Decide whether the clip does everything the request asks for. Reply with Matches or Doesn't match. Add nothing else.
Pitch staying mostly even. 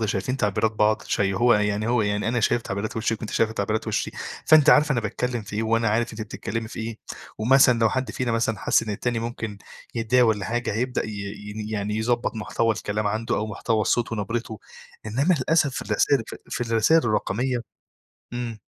Matches